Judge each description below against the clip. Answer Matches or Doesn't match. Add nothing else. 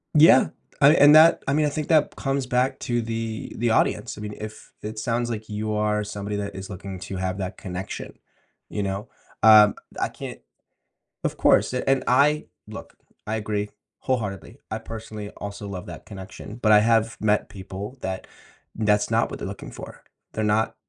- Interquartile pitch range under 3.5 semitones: Matches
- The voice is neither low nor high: Doesn't match